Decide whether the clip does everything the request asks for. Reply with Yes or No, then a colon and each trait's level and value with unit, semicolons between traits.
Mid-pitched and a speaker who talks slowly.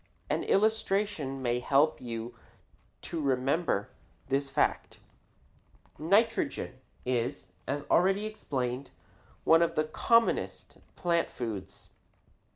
Yes: medium, 145 Hz; slow, 95 wpm